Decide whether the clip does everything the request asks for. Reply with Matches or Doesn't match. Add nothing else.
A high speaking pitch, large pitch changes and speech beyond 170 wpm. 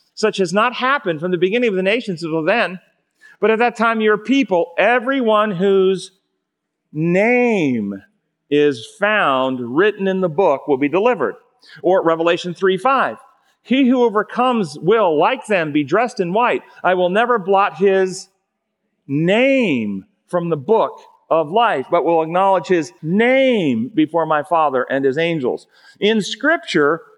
Doesn't match